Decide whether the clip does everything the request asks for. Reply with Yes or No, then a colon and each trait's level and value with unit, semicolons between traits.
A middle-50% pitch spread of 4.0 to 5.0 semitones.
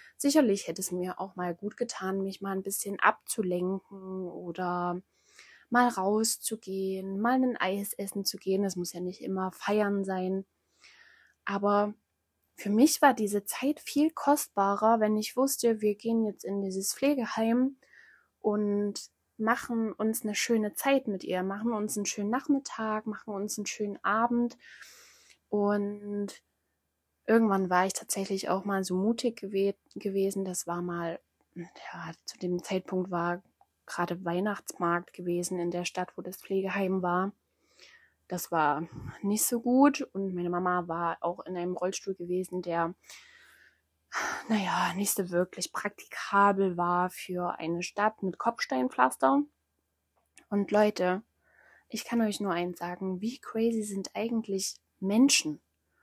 No: average, 3.3 semitones